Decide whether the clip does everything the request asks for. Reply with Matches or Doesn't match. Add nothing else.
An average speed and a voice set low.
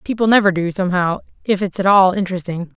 Doesn't match